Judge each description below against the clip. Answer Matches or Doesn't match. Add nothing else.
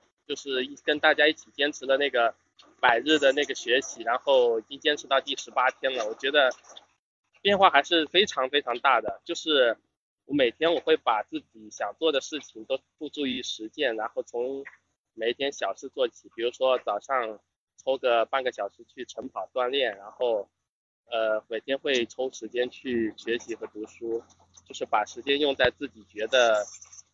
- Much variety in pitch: Matches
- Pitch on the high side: Doesn't match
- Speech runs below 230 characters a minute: Doesn't match